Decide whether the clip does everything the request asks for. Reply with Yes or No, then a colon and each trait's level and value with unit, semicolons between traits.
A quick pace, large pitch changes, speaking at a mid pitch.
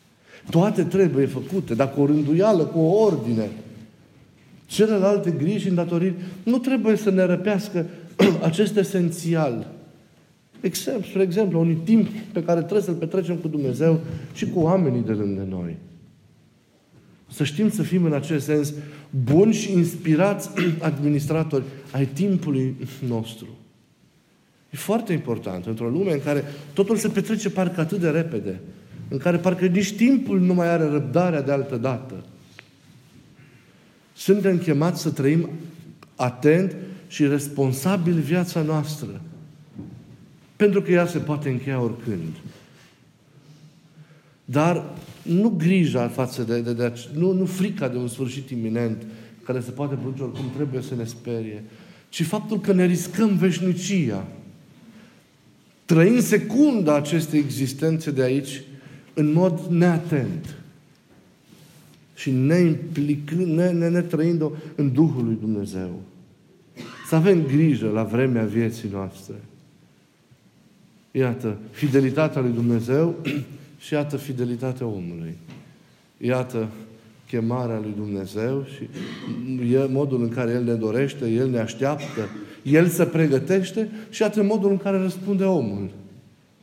No: average, 130 wpm; wide, 5.7 semitones; medium, 150 Hz